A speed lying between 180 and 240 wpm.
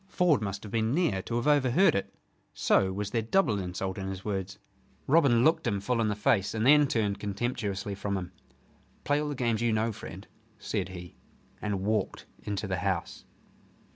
Yes: average, 190 wpm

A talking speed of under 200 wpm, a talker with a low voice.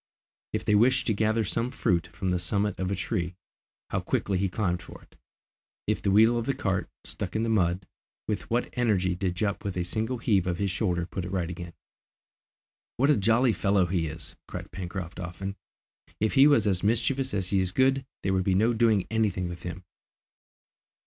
No: fast, 205 wpm; low, 100 Hz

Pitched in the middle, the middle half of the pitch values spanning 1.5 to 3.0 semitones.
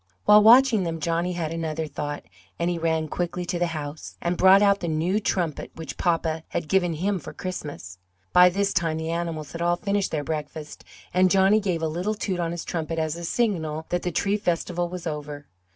Yes: medium, 170 Hz; narrow, 2.6 semitones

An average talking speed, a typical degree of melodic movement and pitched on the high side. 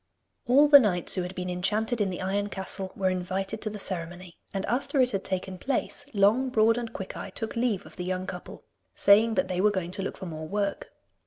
No: fast, 225 wpm; average, 3.3 semitones; high, 195 Hz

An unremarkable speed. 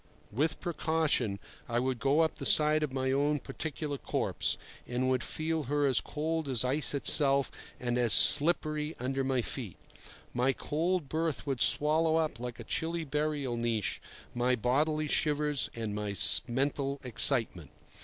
Yes: average, 155 wpm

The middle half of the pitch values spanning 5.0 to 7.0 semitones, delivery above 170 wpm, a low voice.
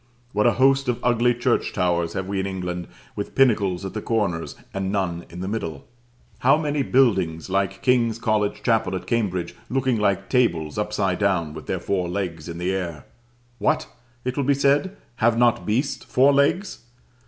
Yes: wide, 5.4 semitones; average, 180 wpm; low, 105 Hz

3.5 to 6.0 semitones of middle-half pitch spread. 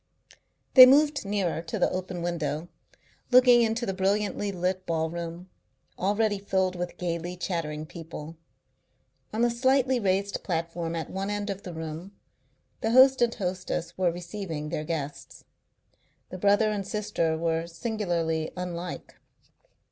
Yes: average, 3.8 semitones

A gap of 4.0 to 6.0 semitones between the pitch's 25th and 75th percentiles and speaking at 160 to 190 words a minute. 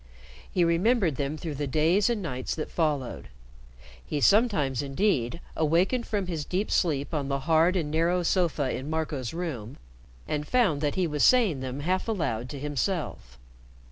Yes: average, 4.4 semitones; average, 165 wpm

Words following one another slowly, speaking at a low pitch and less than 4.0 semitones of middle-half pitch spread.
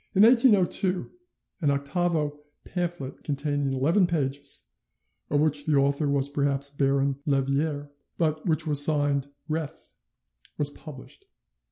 No: slow, 120 wpm; medium, 145 Hz; narrow, 2.4 semitones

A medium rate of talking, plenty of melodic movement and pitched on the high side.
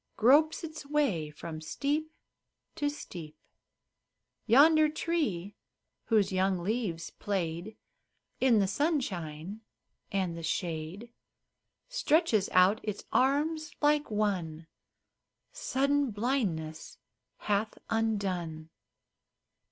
No: slow, 90 wpm; wide, 8.7 semitones; high, 215 Hz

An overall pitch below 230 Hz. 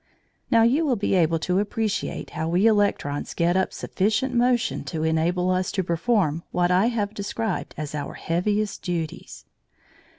Yes: medium, 185 Hz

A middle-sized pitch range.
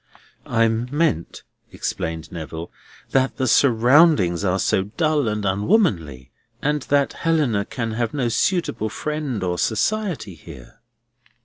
No: wide, 7.7 semitones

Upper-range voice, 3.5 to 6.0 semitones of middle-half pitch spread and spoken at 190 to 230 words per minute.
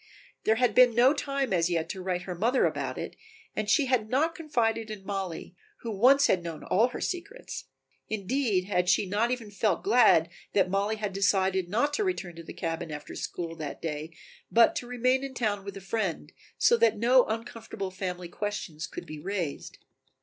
Yes: high, 205 Hz; average, 5.3 semitones; average, 195 wpm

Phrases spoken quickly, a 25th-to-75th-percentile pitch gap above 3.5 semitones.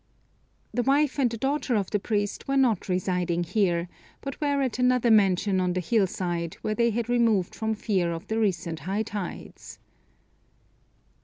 No: average, 170 wpm; average, 4.9 semitones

